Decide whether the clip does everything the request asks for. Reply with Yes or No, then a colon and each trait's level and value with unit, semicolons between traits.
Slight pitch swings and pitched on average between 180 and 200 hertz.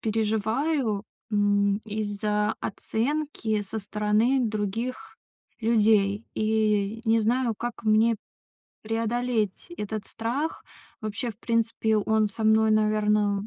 No: narrow, 1.6 semitones; high, 220 Hz